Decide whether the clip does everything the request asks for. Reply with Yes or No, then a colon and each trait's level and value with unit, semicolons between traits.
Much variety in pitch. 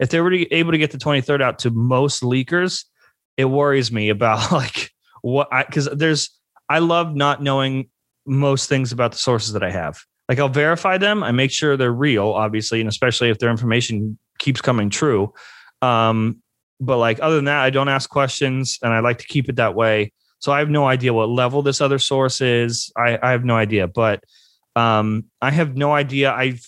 No: average, 3.6 semitones